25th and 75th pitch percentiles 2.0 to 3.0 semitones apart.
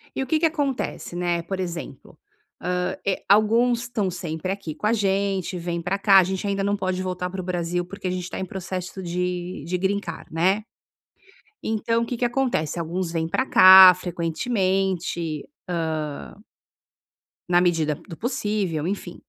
Yes: narrow, 2.6 semitones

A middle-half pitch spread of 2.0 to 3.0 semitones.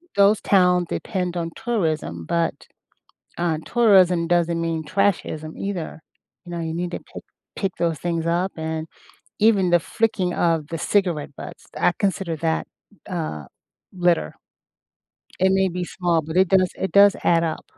Yes: narrow, 2.6 semitones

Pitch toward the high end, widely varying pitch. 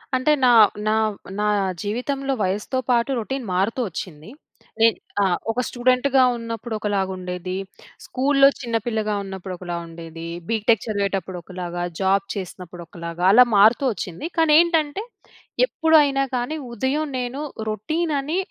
Yes: high, 225 Hz; wide, 6.2 semitones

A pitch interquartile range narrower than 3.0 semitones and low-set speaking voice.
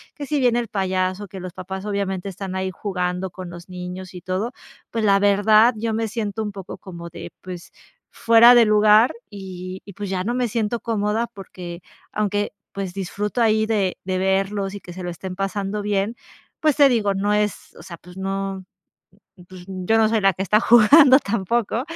No: narrow, 2.6 semitones; high, 200 Hz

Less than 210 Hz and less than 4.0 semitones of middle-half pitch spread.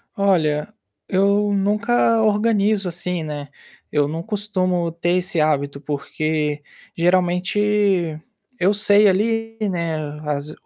No: medium, 185 Hz; average, 4.8 semitones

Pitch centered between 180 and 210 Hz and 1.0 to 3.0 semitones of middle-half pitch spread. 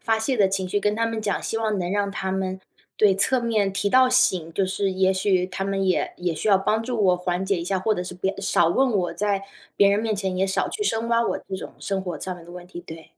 Yes: high, 195 Hz; narrow, 2.5 semitones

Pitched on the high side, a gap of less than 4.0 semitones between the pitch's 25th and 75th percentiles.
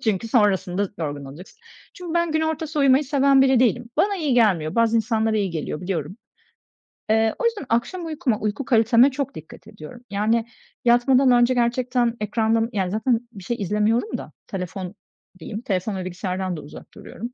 No: high, 225 Hz; average, 5.0 semitones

